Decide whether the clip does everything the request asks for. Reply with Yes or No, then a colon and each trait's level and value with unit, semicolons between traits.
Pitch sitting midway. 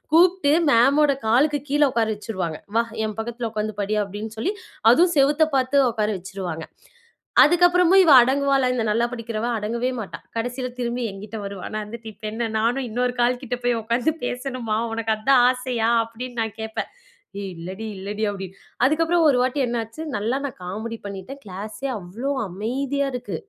No: high, 235 Hz